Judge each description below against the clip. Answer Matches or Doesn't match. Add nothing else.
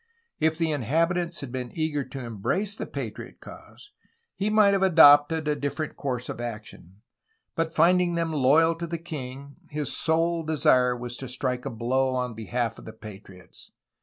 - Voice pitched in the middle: Matches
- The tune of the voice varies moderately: Matches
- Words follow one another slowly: Doesn't match